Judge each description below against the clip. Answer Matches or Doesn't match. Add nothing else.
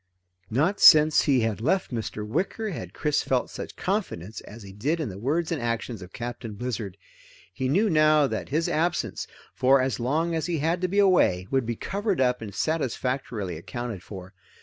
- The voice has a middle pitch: Doesn't match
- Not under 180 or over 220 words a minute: Matches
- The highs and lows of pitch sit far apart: Matches